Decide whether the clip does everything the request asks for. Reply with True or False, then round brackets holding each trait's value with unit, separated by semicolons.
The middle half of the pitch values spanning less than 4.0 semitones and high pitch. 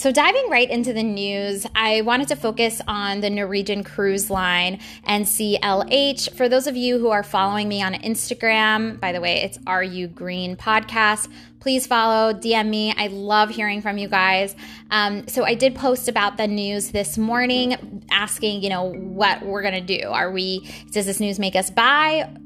True (2.4 semitones; 210 Hz)